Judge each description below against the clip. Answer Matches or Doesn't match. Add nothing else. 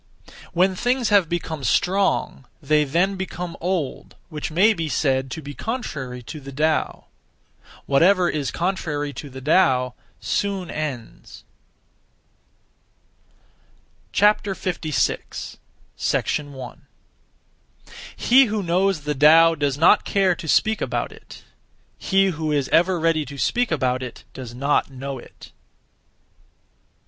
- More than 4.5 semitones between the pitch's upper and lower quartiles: Matches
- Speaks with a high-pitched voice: Doesn't match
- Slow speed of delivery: Matches